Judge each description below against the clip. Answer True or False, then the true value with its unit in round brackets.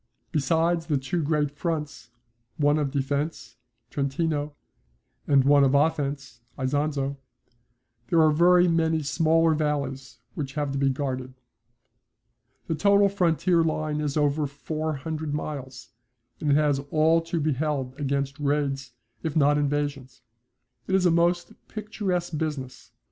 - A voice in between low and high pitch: True (150 Hz)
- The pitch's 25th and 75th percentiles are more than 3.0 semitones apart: False (2.6 semitones)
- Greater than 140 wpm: False (135 wpm)